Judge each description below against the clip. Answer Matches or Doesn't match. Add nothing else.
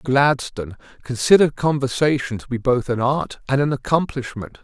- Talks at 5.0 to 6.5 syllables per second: Matches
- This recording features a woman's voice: Doesn't match